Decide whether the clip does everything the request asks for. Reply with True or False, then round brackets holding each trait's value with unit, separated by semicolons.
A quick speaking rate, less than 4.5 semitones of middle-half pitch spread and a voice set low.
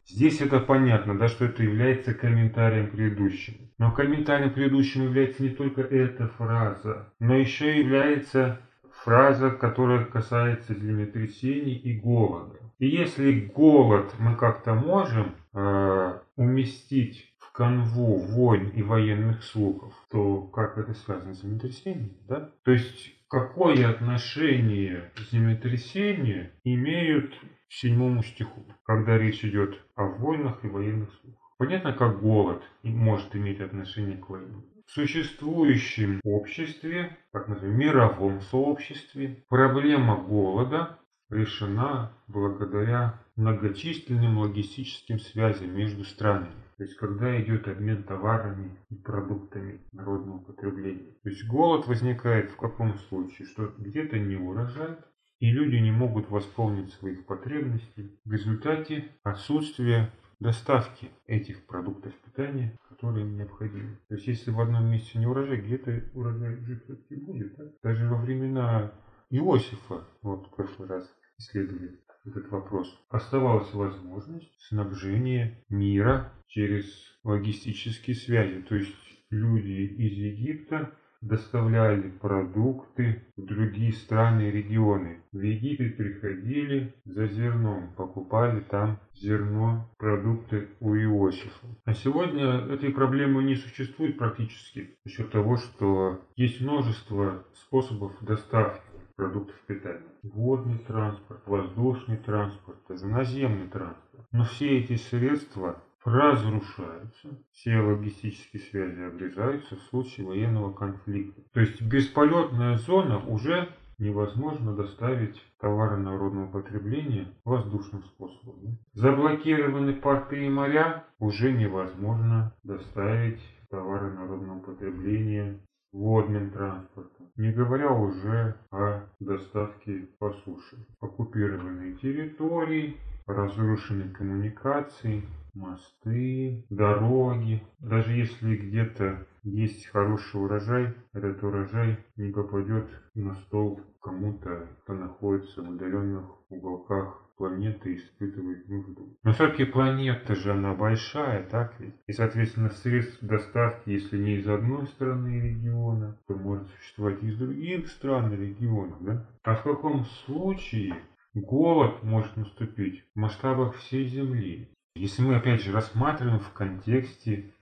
False (115 wpm; 4.1 semitones; 110 Hz)